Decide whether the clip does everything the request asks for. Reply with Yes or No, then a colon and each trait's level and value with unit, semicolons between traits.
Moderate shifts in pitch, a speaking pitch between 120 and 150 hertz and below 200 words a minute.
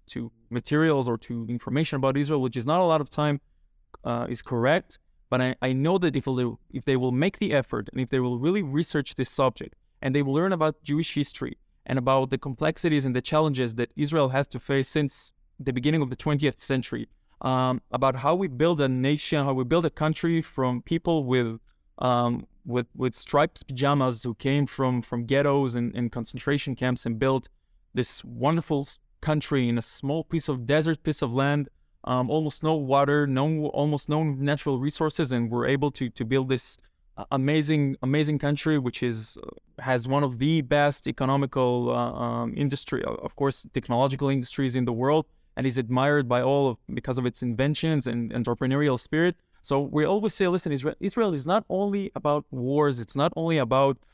Yes: average, 3.0 semitones; medium, 140 Hz; average, 190 wpm